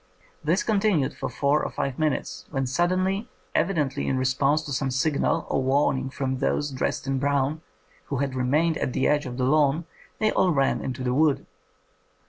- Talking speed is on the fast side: No, average, 185 wpm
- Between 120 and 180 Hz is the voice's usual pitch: Yes, medium, 140 Hz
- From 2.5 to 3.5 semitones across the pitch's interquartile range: Yes, average, 2.9 semitones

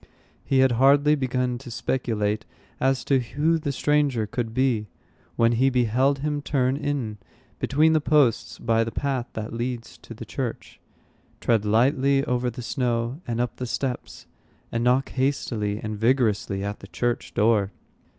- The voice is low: Yes, low, 125 Hz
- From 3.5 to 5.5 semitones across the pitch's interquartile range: No, average, 3.0 semitones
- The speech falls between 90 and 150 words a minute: No, average, 160 wpm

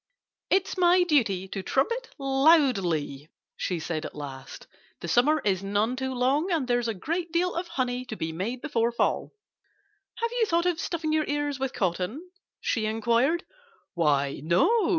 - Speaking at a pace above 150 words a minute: Yes, average, 165 wpm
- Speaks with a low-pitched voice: No, very high, 255 Hz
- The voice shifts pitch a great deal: Yes, wide, 8.9 semitones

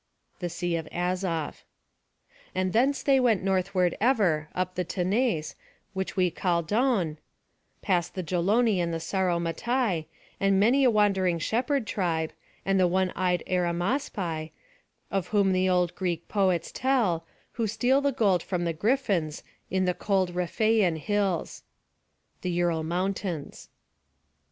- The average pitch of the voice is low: No, medium, 185 Hz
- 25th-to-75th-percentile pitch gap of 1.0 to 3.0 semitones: No, average, 3.5 semitones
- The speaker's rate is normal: No, slow, 115 wpm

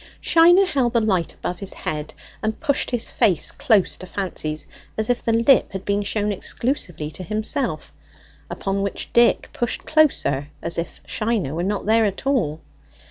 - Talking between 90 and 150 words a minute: No, average, 170 wpm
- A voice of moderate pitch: No, high, 210 Hz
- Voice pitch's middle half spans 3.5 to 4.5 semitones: No, average, 5.2 semitones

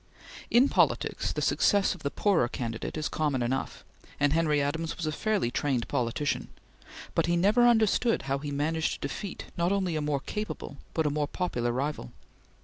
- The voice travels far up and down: No, average, 4.6 semitones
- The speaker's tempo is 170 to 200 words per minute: Yes, average, 180 wpm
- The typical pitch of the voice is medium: Yes, medium, 150 Hz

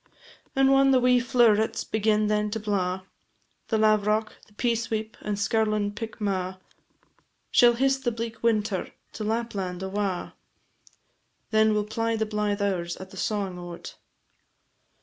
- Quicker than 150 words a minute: No, average, 140 wpm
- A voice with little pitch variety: Yes, narrow, 2.0 semitones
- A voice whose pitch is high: Yes, high, 215 Hz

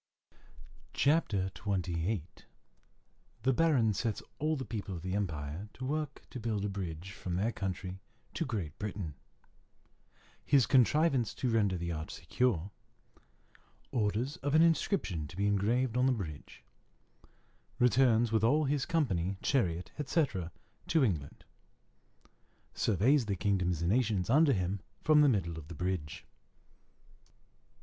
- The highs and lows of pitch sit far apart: Yes, wide, 6.3 semitones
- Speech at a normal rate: No, slow, 130 wpm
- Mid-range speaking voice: No, low, 105 Hz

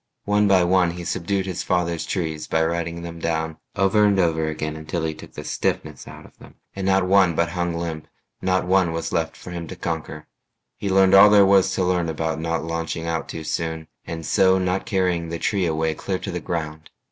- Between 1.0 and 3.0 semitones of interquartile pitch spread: Yes, narrow, 2.6 semitones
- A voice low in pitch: Yes, very low, 85 Hz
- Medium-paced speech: No, fast, 215 wpm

